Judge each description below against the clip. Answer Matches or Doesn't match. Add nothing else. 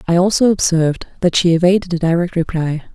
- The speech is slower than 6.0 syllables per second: Doesn't match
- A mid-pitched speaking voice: Matches